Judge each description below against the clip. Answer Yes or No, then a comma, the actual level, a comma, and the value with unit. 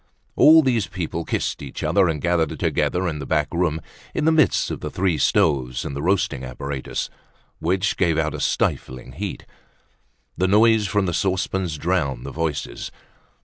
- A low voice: Yes, very low, 85 Hz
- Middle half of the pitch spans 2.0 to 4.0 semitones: No, average, 4.5 semitones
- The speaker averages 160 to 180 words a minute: Yes, average, 170 wpm